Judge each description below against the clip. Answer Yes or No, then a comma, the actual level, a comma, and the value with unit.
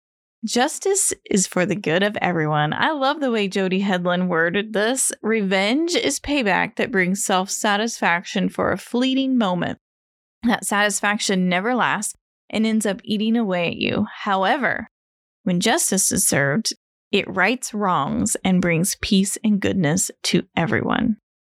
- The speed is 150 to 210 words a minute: No, average, 140 wpm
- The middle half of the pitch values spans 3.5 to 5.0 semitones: Yes, average, 4.3 semitones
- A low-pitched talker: No, high, 205 Hz